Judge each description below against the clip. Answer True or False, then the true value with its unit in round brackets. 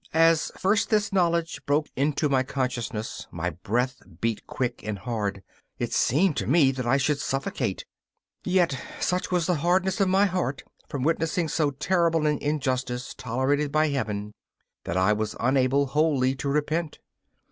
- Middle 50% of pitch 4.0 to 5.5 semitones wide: True (4.7 semitones)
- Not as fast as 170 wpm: True (160 wpm)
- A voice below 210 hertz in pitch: True (140 Hz)